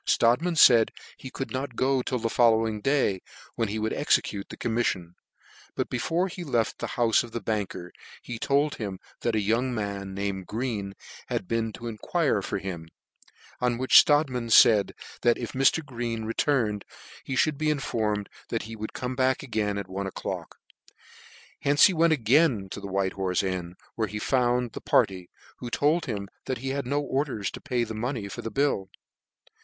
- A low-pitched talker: Yes, low, 115 Hz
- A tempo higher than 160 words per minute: Yes, average, 180 wpm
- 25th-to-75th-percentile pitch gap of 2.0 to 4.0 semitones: No, average, 4.4 semitones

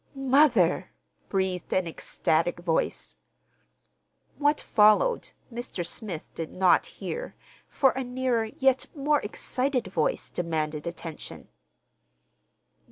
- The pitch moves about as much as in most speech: No, wide, 7.5 semitones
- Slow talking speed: Yes, slow, 100 wpm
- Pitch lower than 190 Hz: No, high, 215 Hz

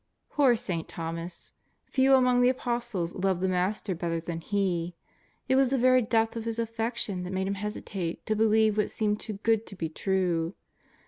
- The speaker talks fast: No, average, 185 wpm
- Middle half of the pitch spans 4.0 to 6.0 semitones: Yes, average, 4.4 semitones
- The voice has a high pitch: Yes, high, 210 Hz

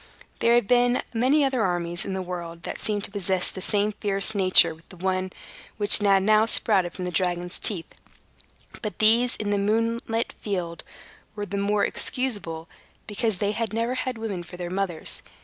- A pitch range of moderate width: Yes, average, 3.6 semitones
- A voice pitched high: Yes, high, 200 Hz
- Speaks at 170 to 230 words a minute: Yes, average, 180 wpm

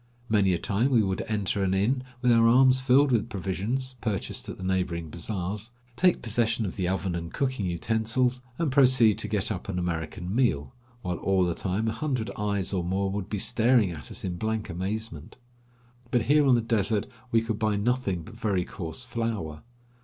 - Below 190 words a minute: No, average, 195 wpm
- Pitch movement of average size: Yes, average, 4.3 semitones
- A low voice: Yes, low, 105 Hz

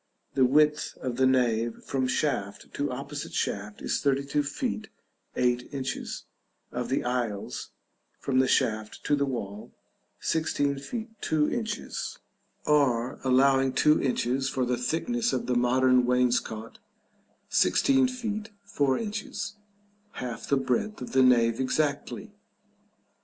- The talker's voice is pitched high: No, low, 130 Hz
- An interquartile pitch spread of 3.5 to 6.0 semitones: No, average, 3.1 semitones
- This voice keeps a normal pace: No, slow, 130 wpm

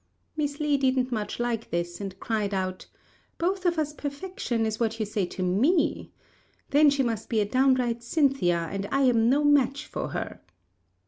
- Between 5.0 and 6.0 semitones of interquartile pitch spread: Yes, average, 5.3 semitones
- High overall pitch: Yes, high, 245 Hz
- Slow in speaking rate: No, average, 180 wpm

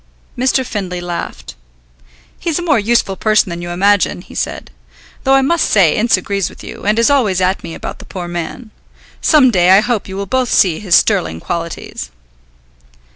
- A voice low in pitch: No, high, 200 Hz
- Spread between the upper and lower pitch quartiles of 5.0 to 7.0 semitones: Yes, wide, 5.5 semitones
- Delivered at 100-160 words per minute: No, average, 185 wpm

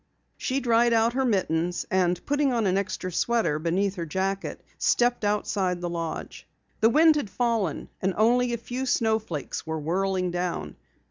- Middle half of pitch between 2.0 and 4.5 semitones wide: No, average, 5.0 semitones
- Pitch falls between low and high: No, high, 200 Hz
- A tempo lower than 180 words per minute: Yes, average, 160 wpm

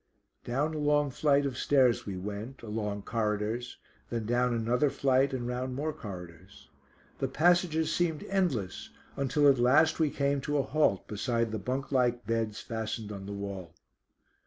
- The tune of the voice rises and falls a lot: No, average, 5.0 semitones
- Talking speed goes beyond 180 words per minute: No, average, 160 wpm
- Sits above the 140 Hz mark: No, low, 125 Hz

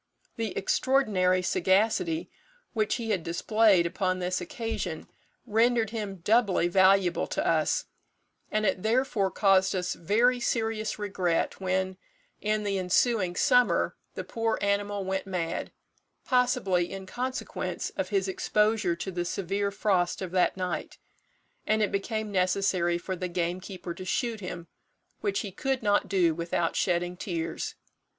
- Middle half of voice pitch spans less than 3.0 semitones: No, average, 3.3 semitones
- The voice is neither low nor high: No, high, 195 Hz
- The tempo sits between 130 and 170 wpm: Yes, average, 140 wpm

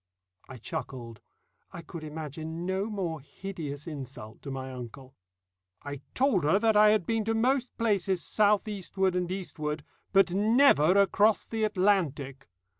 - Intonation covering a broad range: Yes, wide, 6.2 semitones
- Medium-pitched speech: Yes, medium, 180 Hz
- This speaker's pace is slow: No, average, 145 wpm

